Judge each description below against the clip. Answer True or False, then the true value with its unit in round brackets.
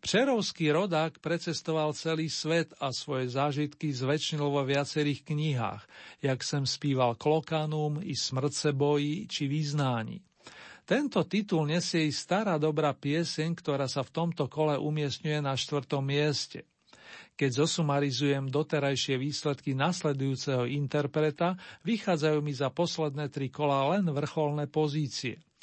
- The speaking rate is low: False (120 wpm)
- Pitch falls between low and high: True (150 Hz)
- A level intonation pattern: True (2.1 semitones)